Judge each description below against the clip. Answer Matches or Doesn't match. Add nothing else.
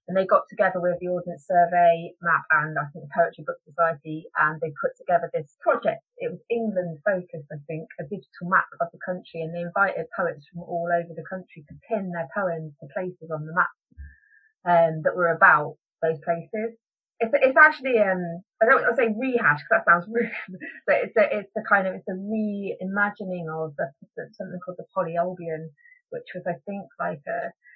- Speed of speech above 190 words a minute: Matches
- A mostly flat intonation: Doesn't match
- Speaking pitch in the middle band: Matches